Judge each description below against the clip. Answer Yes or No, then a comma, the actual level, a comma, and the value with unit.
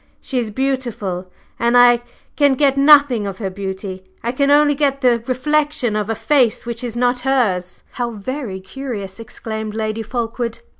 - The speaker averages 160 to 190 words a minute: Yes, average, 165 wpm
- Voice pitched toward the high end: Yes, high, 240 Hz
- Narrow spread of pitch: No, average, 4.0 semitones